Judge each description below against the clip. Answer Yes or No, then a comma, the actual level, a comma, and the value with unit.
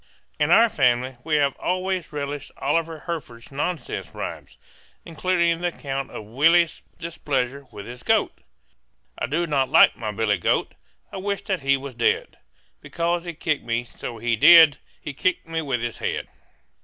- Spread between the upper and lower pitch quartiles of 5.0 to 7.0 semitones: Yes, average, 5.3 semitones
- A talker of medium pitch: Yes, medium, 145 Hz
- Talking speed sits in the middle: Yes, average, 165 wpm